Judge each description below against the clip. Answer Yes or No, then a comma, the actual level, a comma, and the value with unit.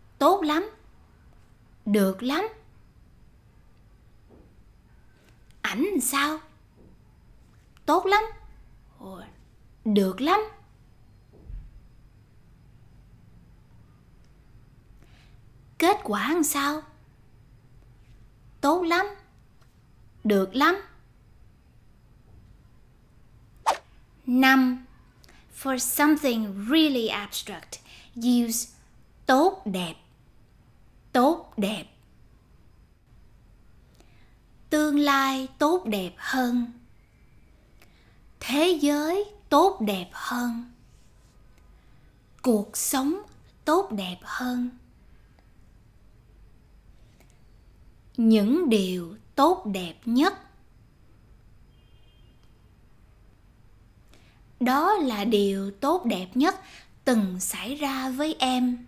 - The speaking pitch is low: No, high, 240 Hz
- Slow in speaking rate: Yes, slow, 60 wpm